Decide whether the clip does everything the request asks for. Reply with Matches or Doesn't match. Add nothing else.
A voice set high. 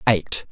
Doesn't match